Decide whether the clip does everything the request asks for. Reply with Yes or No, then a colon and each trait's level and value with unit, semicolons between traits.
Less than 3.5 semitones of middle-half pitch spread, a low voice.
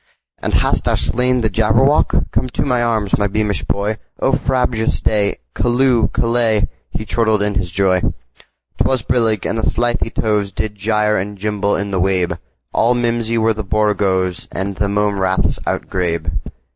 Yes: average, 2.8 semitones; low, 105 Hz